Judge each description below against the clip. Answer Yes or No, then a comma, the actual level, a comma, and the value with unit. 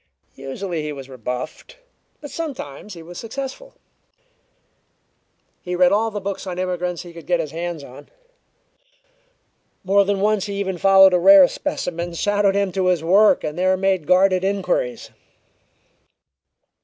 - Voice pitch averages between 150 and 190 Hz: Yes, medium, 185 Hz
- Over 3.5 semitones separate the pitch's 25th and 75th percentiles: No, average, 2.9 semitones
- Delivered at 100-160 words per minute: Yes, average, 145 wpm